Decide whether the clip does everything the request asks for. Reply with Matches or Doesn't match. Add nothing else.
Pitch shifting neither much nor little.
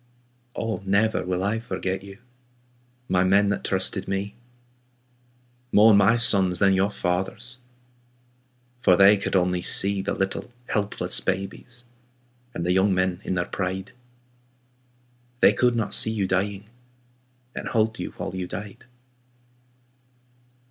Doesn't match